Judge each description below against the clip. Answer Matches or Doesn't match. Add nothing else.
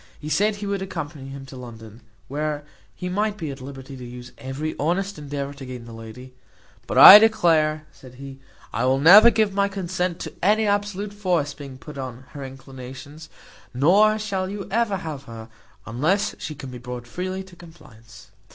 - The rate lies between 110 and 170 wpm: Doesn't match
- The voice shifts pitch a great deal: Matches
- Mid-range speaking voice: Matches